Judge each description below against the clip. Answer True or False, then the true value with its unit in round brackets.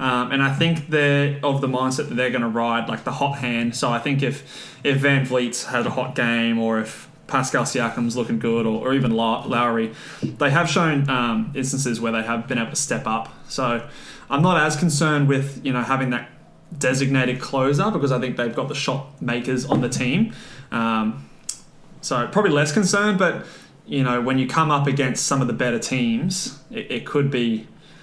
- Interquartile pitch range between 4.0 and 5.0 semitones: False (3.1 semitones)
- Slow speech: False (205 wpm)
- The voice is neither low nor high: False (130 Hz)